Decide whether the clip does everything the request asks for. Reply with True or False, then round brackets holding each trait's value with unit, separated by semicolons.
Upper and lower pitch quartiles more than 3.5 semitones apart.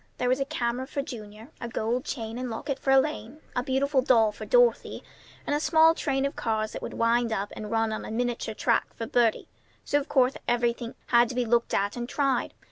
False (3.0 semitones)